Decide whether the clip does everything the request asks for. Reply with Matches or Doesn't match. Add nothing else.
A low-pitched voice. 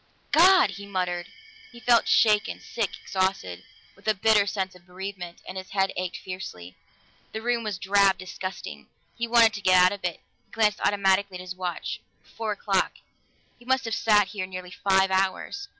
Doesn't match